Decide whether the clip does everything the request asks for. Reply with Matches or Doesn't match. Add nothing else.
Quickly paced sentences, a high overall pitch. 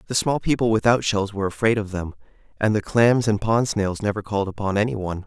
Doesn't match